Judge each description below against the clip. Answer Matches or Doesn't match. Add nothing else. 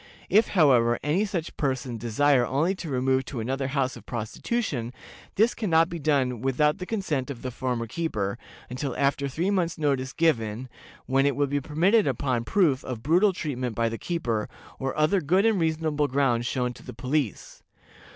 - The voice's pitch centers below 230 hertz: Matches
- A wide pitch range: Doesn't match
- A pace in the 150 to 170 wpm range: Doesn't match